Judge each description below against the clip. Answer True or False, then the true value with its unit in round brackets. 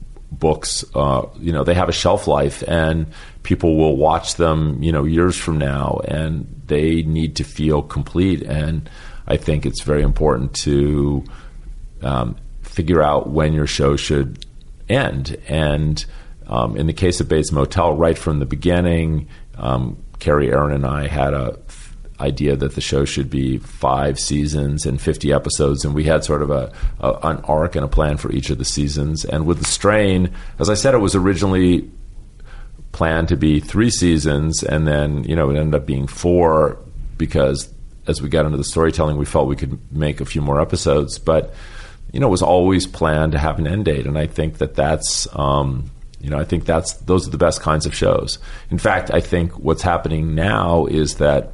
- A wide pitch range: False (2.6 semitones)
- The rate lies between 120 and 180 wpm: False (195 wpm)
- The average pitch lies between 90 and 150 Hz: False (75 Hz)